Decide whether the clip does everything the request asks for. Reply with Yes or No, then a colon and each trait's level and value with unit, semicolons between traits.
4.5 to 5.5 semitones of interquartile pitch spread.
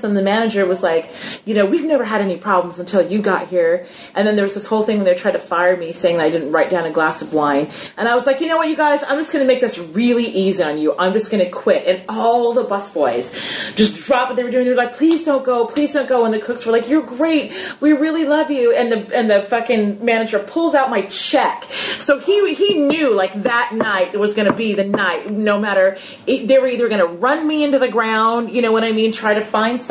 Yes: average, 4.9 semitones